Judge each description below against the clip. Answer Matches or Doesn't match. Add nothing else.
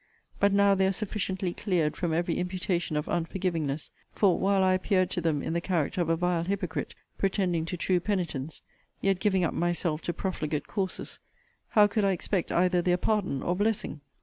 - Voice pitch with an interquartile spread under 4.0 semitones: Matches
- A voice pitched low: Doesn't match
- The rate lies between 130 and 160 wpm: Doesn't match